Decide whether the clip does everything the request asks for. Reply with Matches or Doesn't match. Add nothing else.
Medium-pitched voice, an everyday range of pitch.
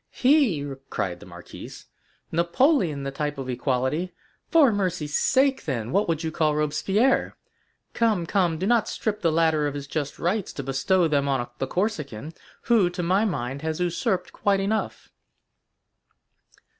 Doesn't match